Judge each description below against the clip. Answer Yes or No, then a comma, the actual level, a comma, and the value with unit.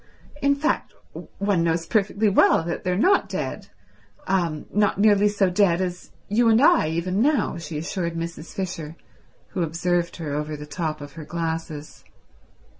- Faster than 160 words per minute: No, average, 150 wpm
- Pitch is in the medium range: Yes, medium, 175 Hz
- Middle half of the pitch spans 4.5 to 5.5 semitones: No, average, 3.8 semitones